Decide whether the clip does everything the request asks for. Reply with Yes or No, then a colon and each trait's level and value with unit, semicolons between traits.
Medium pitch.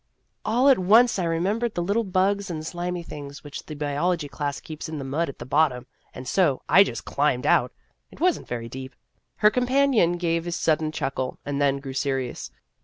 Yes: medium, 165 Hz